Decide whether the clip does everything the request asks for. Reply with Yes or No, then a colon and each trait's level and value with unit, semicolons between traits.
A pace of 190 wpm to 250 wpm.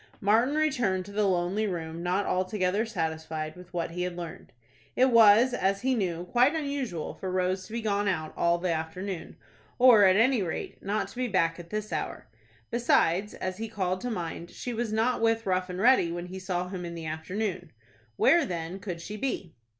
Yes: average, 200 wpm